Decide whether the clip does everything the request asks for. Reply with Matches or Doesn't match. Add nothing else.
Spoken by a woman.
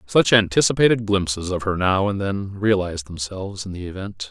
Doesn't match